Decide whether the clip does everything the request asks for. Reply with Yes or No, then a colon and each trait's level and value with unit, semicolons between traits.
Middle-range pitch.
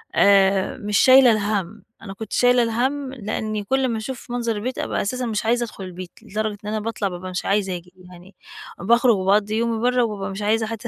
No: high, 215 Hz